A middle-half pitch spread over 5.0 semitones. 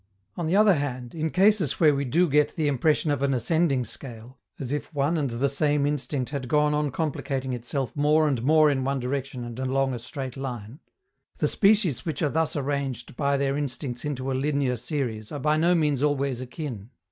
No: average, 2.8 semitones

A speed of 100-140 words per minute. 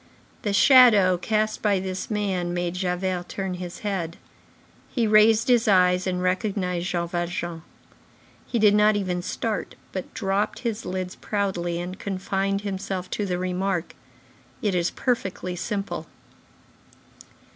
Yes: slow, 135 wpm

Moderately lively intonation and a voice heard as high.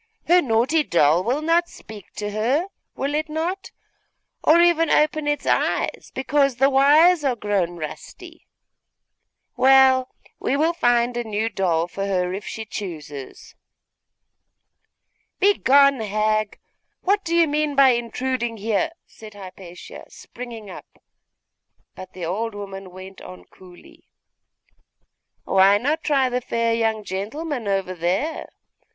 No: wide, 6.8 semitones; high, 235 Hz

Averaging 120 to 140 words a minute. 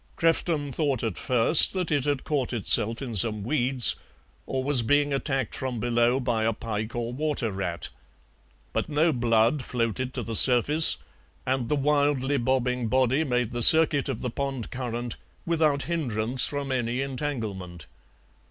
No: average, 155 wpm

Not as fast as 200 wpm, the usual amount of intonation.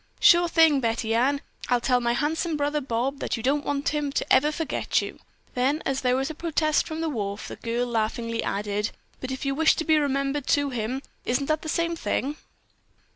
No: fast, 205 wpm; average, 4.0 semitones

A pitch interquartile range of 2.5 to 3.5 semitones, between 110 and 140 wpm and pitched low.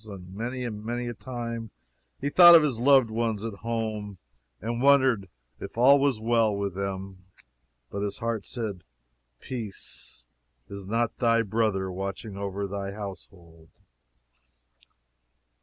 Yes: average, 3.2 semitones; slow, 135 wpm; low, 110 Hz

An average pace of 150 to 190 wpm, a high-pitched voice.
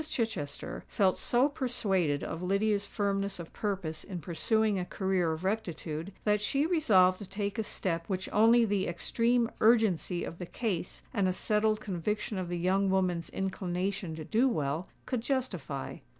Yes: average, 165 wpm; high, 195 Hz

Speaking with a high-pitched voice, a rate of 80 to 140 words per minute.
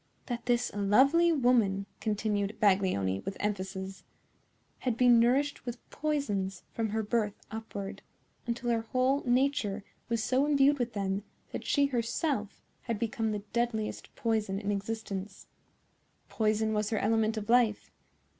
Yes: high, 220 Hz; slow, 135 wpm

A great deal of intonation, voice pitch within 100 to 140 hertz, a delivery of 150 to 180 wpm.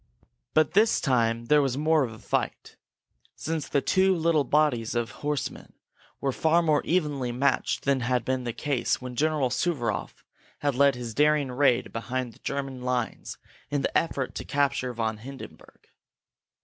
No: average, 3.5 semitones; low, 135 Hz; average, 160 wpm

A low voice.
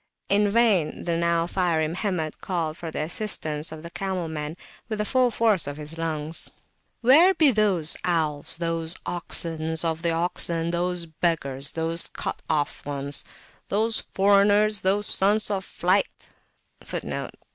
No: medium, 170 Hz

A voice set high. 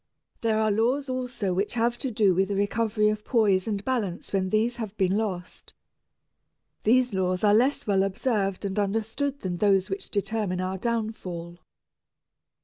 Yes: high, 210 Hz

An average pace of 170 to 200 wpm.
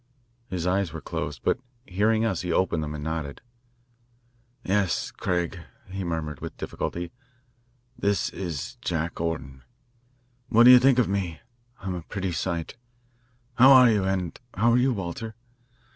No: average, 150 wpm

